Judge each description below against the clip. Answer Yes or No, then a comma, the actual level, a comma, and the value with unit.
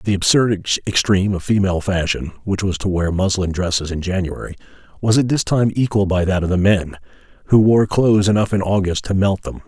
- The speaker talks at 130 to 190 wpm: No, fast, 205 wpm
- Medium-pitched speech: No, very low, 95 Hz